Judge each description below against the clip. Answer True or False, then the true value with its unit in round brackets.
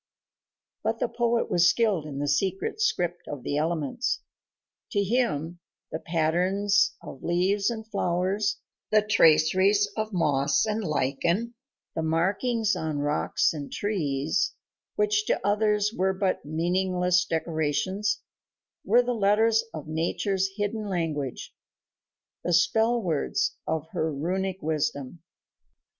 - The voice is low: False (185 Hz)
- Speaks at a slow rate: True (120 wpm)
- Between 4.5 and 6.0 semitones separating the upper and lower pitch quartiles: True (4.8 semitones)